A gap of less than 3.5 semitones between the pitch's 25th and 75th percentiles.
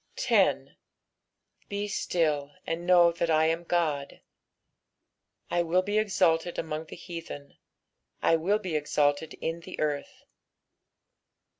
Yes: narrow, 2.4 semitones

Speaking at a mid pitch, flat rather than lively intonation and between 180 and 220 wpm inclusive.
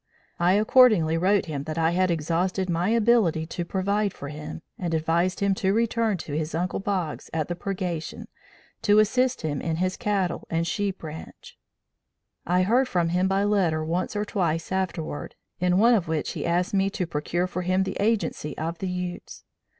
No: medium, 180 Hz; average, 3.3 semitones; average, 185 wpm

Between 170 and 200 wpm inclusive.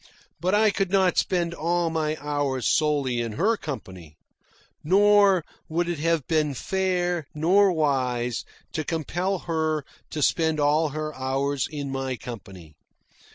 No: average, 140 wpm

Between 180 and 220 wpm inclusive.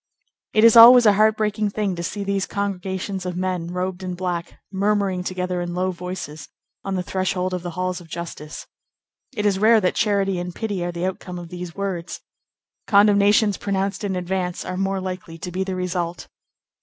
Yes: average, 190 wpm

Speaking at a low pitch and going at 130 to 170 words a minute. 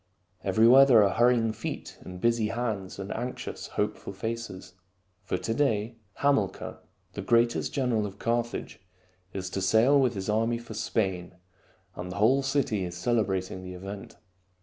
Yes: low, 110 Hz; average, 150 wpm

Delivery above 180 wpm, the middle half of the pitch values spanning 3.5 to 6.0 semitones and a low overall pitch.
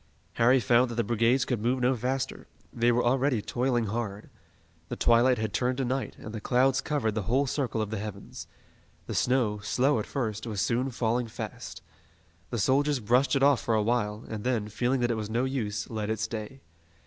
No: fast, 205 wpm; average, 2.9 semitones; low, 120 Hz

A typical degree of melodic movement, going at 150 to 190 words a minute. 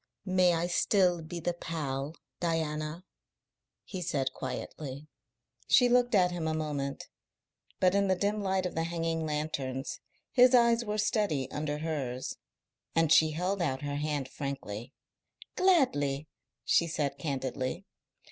No: average, 4.5 semitones; average, 140 wpm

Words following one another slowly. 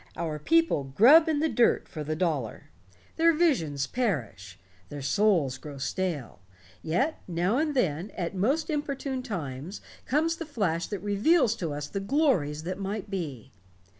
No: average, 155 wpm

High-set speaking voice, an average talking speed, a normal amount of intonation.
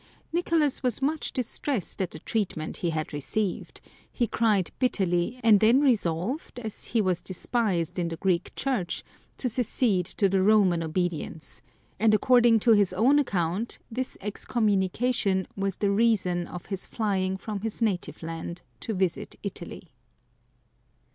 Yes: high, 200 Hz; average, 150 wpm; average, 4.7 semitones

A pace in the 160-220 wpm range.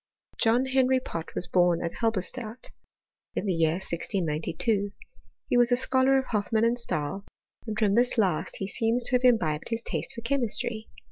Yes: average, 175 wpm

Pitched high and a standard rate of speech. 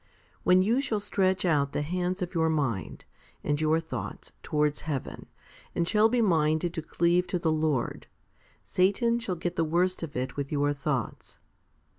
No: medium, 165 Hz; average, 170 wpm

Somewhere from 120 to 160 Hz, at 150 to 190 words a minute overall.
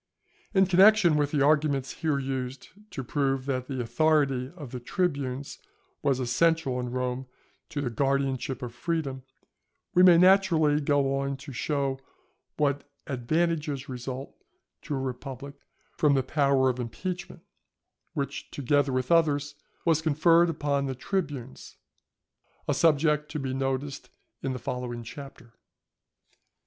No: medium, 140 Hz; slow, 135 wpm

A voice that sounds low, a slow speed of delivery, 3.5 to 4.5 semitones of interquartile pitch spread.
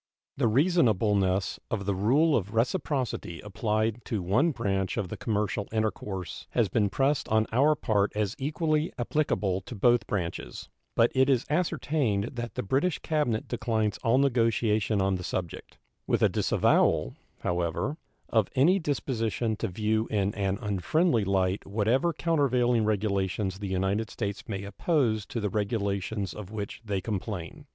No: low, 110 Hz; average, 150 wpm; average, 4.2 semitones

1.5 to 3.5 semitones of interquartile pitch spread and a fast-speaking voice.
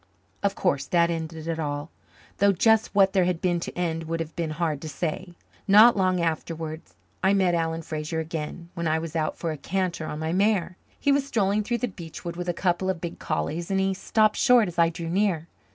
Yes: average, 2.9 semitones; fast, 225 wpm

